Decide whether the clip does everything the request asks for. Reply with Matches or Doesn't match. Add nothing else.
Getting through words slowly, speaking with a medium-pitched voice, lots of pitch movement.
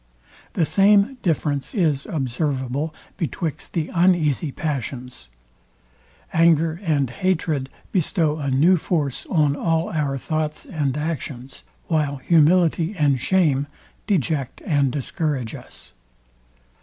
Doesn't match